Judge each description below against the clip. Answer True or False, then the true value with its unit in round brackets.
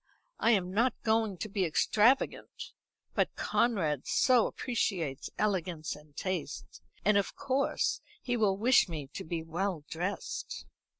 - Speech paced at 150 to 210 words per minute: False (135 wpm)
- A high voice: True (195 Hz)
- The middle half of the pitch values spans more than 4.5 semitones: True (5.6 semitones)